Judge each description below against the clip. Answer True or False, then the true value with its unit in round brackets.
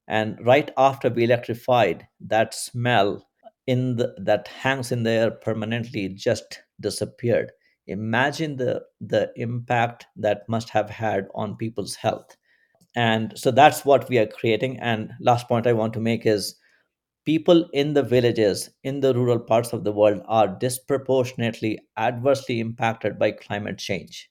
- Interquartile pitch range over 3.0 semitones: False (2.6 semitones)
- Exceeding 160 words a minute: False (150 wpm)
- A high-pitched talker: False (115 Hz)